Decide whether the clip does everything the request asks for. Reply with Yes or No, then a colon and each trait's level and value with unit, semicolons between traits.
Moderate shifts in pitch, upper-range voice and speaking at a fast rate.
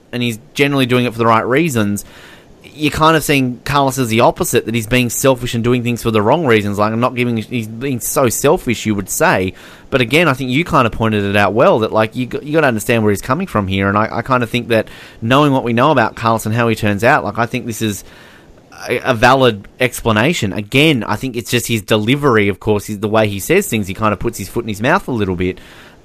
No: average, 3.3 semitones; low, 115 Hz; fast, 265 wpm